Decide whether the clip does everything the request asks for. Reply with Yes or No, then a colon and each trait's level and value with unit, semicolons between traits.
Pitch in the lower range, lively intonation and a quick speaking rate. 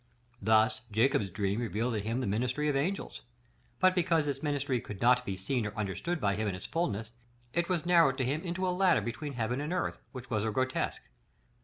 Yes: low, 125 Hz; wide, 6.3 semitones; fast, 210 wpm